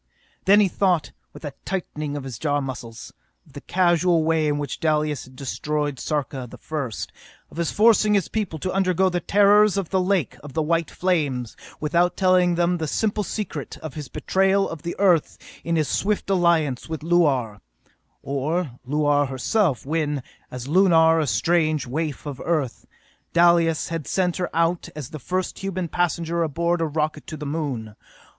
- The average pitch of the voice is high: No, medium, 160 Hz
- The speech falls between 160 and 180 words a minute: Yes, average, 175 wpm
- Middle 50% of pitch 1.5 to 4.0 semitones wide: Yes, average, 3.6 semitones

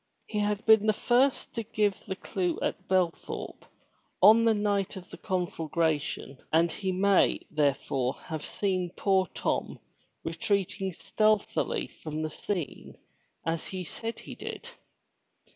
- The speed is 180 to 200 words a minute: No, slow, 135 wpm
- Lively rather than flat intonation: No, average, 4.1 semitones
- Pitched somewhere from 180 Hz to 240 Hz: Yes, high, 190 Hz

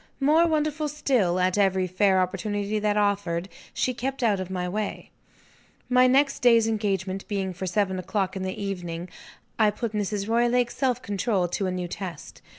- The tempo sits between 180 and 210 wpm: No, average, 170 wpm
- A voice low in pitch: No, high, 205 Hz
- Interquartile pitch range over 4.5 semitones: No, average, 4.2 semitones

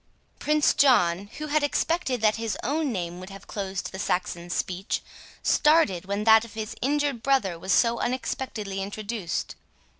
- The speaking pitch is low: No, high, 220 Hz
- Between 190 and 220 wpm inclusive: No, average, 155 wpm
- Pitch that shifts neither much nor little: No, wide, 5.9 semitones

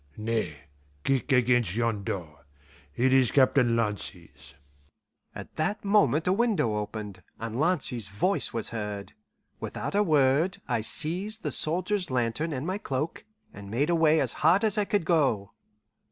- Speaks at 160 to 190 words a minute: No, average, 150 wpm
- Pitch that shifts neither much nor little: No, wide, 7.6 semitones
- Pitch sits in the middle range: No, low, 130 Hz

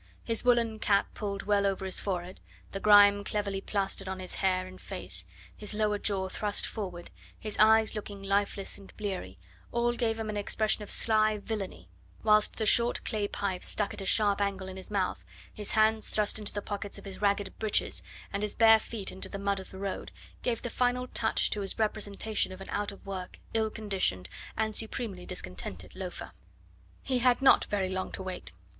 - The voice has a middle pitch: No, high, 205 Hz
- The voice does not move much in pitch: Yes, narrow, 2.1 semitones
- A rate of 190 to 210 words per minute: Yes, average, 195 wpm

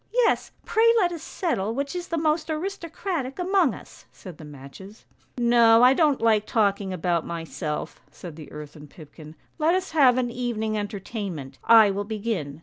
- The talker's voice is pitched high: Yes, high, 225 Hz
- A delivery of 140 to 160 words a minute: No, average, 185 wpm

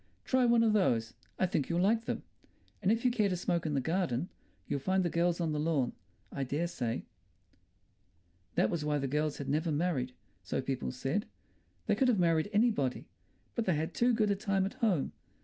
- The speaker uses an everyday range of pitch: No, wide, 6.1 semitones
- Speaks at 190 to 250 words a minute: Yes, fast, 205 wpm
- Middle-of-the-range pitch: Yes, medium, 170 Hz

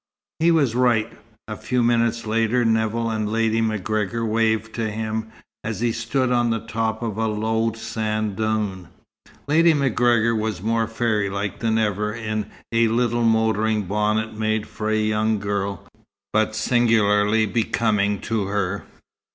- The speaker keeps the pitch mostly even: Yes, narrow, 1.3 semitones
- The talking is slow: No, average, 145 wpm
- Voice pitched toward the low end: Yes, low, 110 Hz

